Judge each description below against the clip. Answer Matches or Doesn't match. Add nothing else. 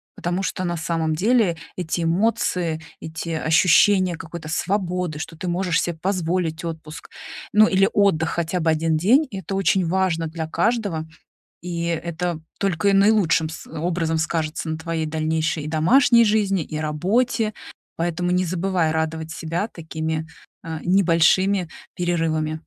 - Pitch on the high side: Doesn't match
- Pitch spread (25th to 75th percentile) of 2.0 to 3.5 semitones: Matches